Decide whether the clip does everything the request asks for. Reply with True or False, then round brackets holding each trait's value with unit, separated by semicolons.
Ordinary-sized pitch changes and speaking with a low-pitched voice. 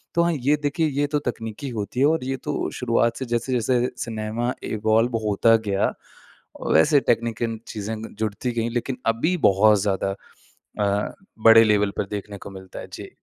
True (3.1 semitones; 115 Hz)